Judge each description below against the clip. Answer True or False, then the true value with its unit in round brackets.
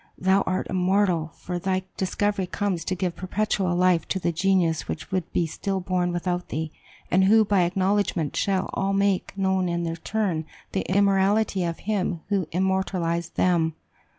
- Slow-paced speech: False (165 wpm)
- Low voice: False (185 Hz)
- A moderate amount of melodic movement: False (2.1 semitones)